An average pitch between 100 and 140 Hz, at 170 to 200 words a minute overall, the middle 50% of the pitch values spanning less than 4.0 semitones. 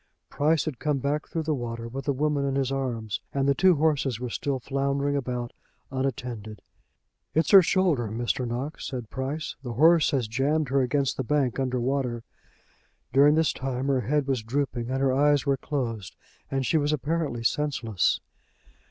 Yes: low, 135 Hz; average, 180 wpm; average, 3.0 semitones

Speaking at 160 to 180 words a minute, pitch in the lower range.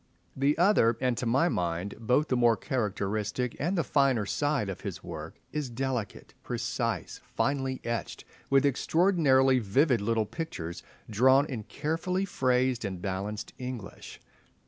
No: average, 140 wpm; low, 125 Hz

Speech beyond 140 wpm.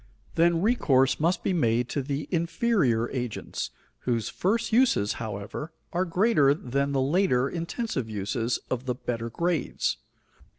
No: slow, 135 wpm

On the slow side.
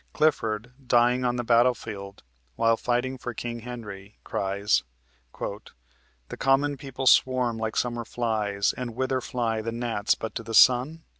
No: average, 145 wpm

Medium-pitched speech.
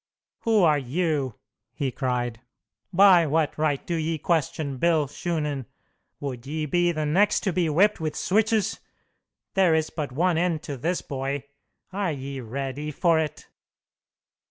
Yes: medium, 155 Hz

